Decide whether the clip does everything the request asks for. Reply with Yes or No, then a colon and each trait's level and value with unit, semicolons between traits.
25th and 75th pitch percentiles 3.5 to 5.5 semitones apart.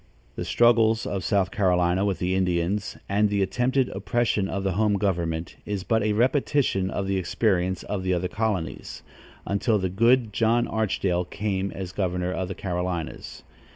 No: average, 3.0 semitones